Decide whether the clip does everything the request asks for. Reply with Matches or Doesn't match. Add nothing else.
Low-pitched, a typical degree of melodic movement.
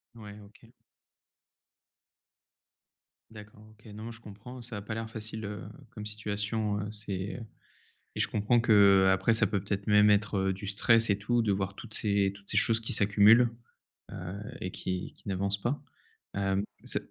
Doesn't match